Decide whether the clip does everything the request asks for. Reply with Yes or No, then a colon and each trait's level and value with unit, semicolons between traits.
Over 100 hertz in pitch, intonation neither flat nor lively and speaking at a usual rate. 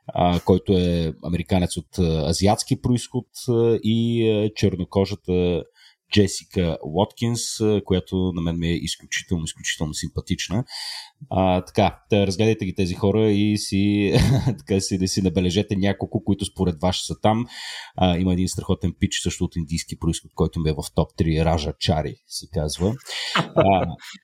No: very low, 95 Hz; average, 3.5 semitones; average, 145 wpm